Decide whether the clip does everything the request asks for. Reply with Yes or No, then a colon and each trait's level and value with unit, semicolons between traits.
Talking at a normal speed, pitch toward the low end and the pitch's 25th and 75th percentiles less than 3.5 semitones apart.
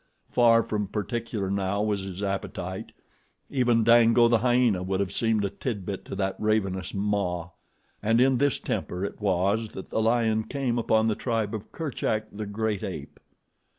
Yes: average, 165 wpm; low, 110 Hz; average, 2.9 semitones